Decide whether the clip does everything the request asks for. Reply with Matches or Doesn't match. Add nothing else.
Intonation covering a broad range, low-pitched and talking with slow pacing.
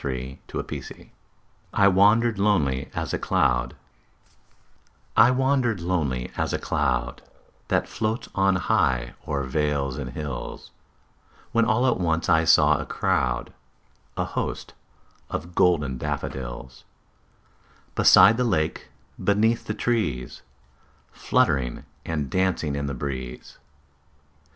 Matches